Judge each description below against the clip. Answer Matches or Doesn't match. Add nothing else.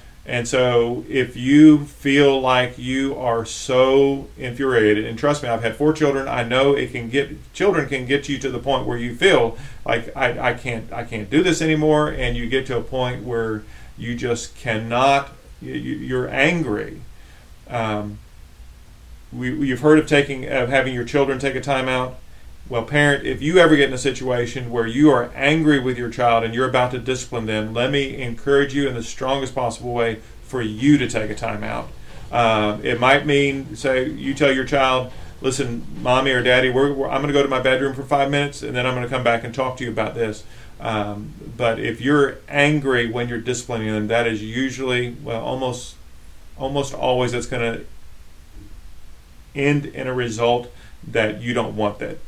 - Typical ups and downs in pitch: Matches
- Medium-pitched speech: Doesn't match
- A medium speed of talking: Matches